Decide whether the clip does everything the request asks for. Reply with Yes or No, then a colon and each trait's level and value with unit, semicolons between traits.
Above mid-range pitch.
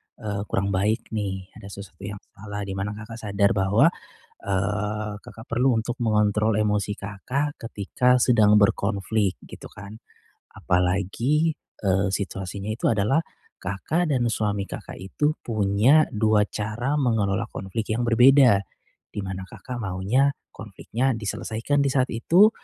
No: low, 105 Hz